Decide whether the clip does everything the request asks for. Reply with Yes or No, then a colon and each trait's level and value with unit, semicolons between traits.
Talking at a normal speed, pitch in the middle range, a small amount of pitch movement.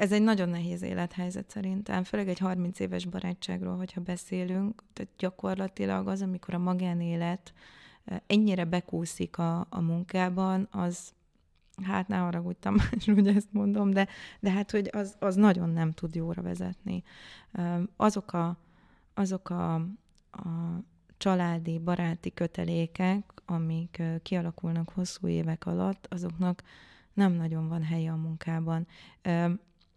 Yes: average, 125 wpm; medium, 180 Hz; narrow, 2.3 semitones